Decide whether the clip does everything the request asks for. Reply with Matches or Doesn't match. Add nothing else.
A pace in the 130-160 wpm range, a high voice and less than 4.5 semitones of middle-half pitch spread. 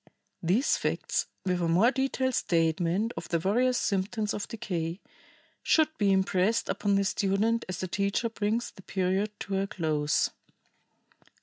Matches